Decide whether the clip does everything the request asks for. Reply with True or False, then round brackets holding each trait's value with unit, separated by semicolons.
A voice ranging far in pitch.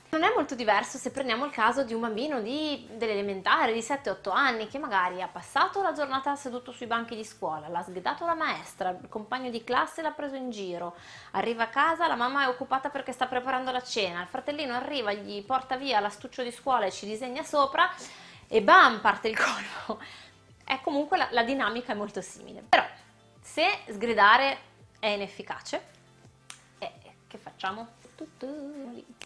False (4.7 semitones)